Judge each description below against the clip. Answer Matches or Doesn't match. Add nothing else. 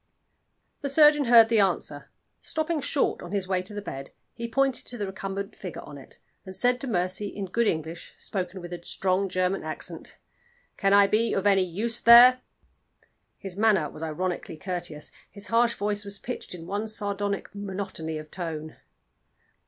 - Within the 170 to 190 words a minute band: Matches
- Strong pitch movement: Doesn't match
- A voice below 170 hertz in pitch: Doesn't match